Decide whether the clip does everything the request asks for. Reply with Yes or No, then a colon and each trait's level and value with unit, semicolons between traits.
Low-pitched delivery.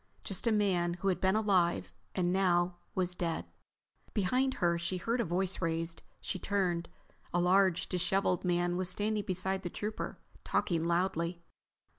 No: medium, 180 Hz